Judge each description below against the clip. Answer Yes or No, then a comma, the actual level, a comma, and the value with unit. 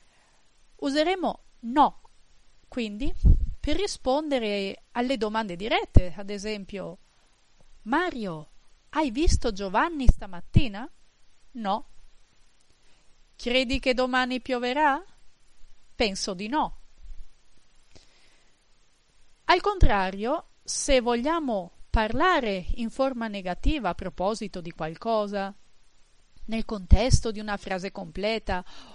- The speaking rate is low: Yes, slow, 85 wpm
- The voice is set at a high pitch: Yes, high, 225 Hz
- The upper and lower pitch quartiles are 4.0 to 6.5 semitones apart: Yes, wide, 5.4 semitones